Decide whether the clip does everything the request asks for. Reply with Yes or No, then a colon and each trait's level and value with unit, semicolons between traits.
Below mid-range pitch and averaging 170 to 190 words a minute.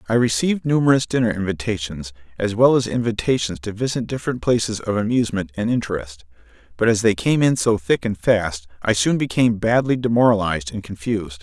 Yes: low, 110 Hz; average, 175 wpm